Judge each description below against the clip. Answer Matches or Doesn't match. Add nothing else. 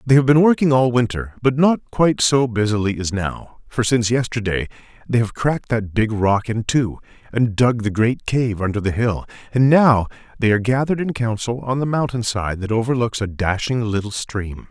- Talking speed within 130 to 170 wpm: Doesn't match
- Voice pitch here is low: Matches